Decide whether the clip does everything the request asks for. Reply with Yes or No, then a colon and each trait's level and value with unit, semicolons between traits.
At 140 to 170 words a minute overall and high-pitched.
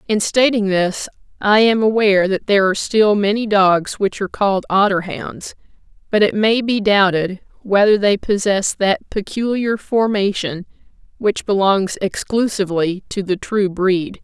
Yes: average, 150 wpm; high, 200 Hz